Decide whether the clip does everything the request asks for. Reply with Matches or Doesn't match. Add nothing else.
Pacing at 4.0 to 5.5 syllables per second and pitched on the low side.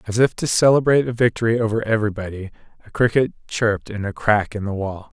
Doesn't match